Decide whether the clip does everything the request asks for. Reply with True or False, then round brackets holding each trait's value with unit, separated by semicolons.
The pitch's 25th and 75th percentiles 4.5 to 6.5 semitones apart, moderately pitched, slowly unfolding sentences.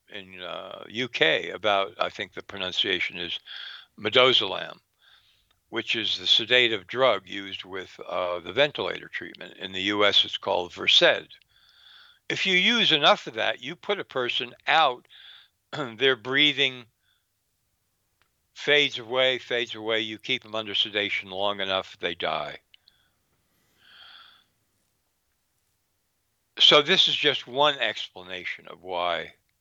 False (5.6 semitones; 110 Hz; 125 wpm)